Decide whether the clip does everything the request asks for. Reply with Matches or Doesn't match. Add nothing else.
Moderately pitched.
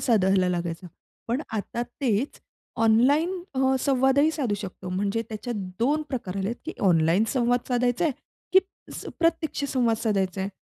Doesn't match